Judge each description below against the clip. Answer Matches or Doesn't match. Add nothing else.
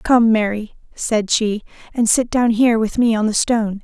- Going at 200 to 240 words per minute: Matches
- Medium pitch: Doesn't match